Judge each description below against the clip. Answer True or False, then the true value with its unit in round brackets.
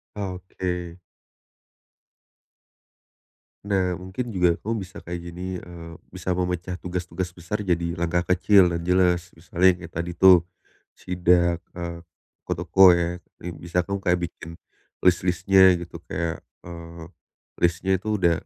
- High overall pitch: False (90 Hz)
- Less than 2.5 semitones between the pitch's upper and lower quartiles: True (1.3 semitones)